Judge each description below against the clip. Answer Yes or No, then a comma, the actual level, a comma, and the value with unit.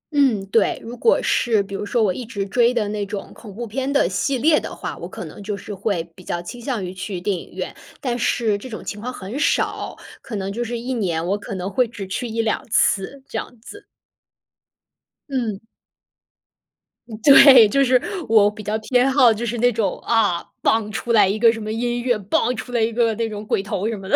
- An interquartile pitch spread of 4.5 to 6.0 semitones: No, average, 3.2 semitones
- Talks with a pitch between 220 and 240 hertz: Yes, high, 225 Hz